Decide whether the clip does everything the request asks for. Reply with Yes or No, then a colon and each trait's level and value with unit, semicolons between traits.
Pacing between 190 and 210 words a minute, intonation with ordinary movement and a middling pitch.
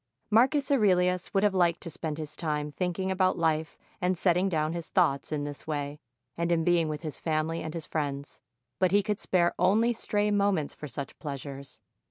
Yes: average, 195 wpm; average, 3.6 semitones; medium, 170 Hz